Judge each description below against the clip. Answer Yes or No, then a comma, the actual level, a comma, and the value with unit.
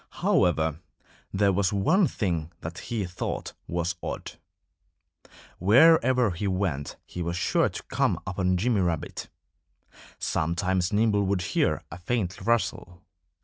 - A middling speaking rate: No, slow, 125 wpm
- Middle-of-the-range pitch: No, very low, 95 Hz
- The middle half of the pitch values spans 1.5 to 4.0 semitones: Yes, average, 3.1 semitones